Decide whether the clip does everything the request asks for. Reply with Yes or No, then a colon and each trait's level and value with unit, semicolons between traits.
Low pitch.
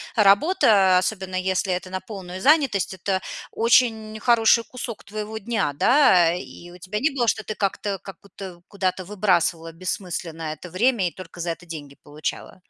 No: high, 190 Hz